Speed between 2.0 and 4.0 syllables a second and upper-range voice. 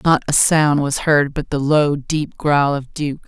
No: 3.9 syllables/s; medium, 145 Hz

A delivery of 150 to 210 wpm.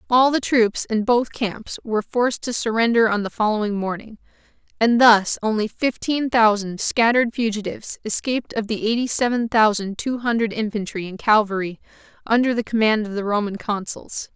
Yes: average, 165 wpm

